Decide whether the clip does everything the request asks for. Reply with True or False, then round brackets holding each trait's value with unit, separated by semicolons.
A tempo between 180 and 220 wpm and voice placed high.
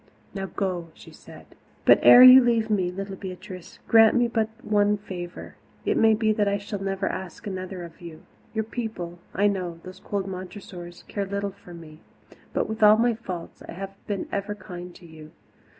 True (195 wpm; 195 Hz)